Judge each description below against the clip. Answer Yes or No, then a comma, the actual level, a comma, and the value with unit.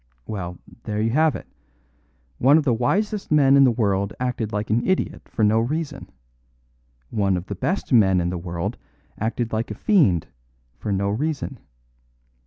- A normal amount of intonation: No, wide, 5.8 semitones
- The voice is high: No, low, 110 Hz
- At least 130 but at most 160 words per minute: No, average, 170 wpm